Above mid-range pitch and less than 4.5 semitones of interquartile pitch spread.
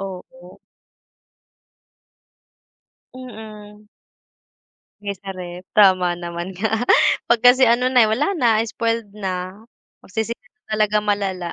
Yes: high, 210 Hz; average, 3.6 semitones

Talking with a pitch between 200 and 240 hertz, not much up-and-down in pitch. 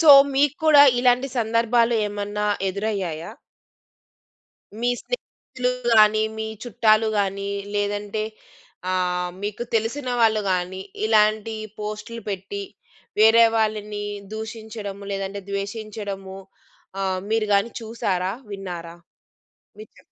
Yes: high, 210 Hz; narrow, 2.2 semitones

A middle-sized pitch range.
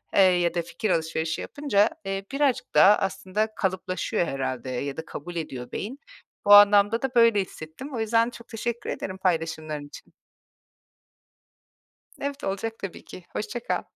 No: wide, 5.7 semitones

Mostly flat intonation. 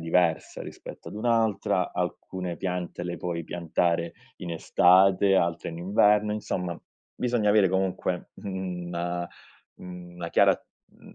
Yes: narrow, 2.0 semitones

